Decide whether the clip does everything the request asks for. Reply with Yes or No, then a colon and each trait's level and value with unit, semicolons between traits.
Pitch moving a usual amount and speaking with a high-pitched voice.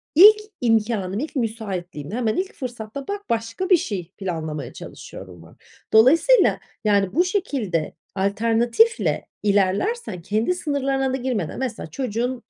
No: wide, 6.1 semitones; high, 230 Hz